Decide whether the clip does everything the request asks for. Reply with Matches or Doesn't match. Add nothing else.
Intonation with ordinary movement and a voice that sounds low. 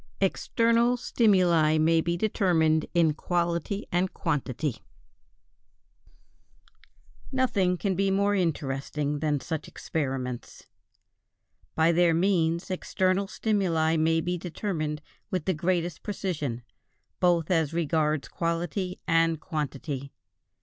Doesn't match